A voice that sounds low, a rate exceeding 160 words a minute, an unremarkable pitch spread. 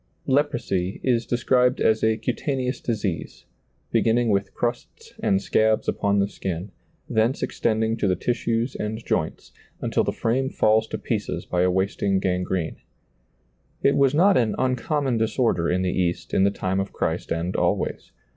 No: low, 110 Hz; average, 155 wpm; average, 4.4 semitones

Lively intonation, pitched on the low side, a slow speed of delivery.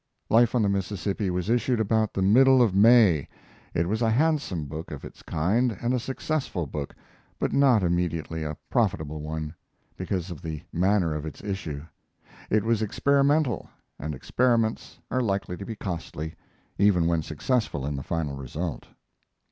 No: wide, 6.4 semitones; very low, 95 Hz; average, 165 wpm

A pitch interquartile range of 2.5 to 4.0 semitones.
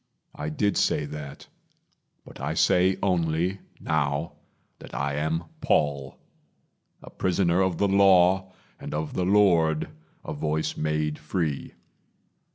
Yes: average, 3.6 semitones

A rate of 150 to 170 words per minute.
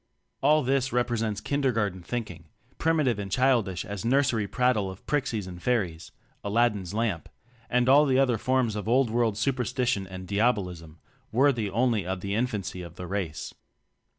Yes: average, 160 wpm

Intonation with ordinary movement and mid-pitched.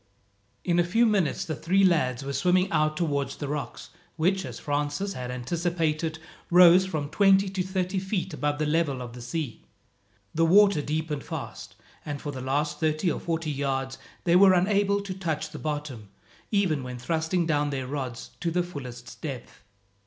Yes: average, 4.4 semitones; medium, 155 Hz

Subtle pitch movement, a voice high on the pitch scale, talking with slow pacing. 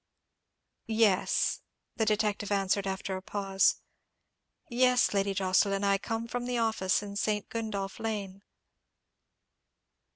Yes: narrow, 2.3 semitones; high, 205 Hz; slow, 110 wpm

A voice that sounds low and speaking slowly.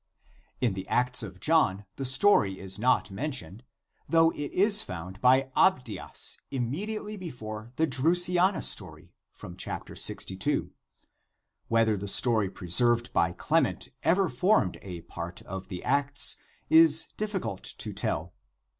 Yes: low, 125 Hz; slow, 130 wpm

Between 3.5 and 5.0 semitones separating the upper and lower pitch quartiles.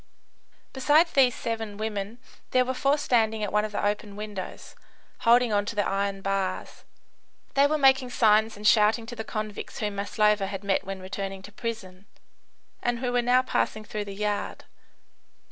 No: average, 3.1 semitones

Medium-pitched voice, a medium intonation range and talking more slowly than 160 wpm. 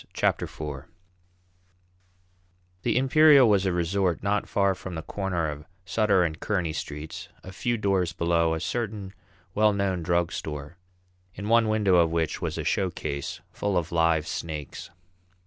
No: very low, 90 Hz; average, 3.8 semitones; average, 150 wpm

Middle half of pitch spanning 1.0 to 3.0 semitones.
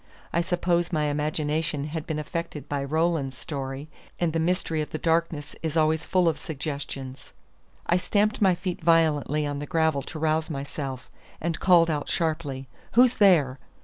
Yes: narrow, 2.5 semitones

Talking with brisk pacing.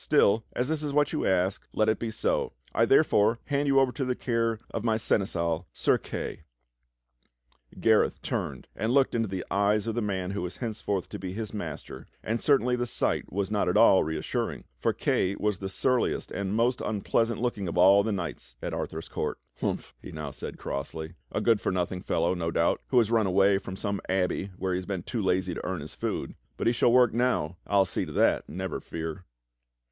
Yes: fast, 210 wpm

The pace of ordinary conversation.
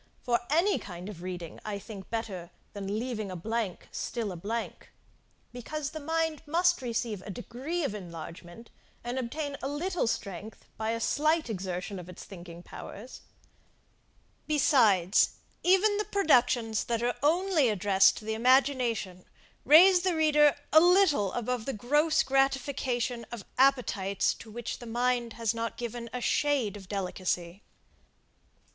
Yes: average, 145 wpm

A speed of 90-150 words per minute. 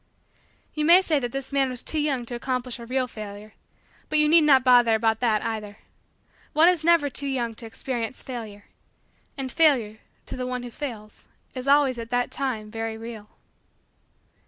No: average, 180 wpm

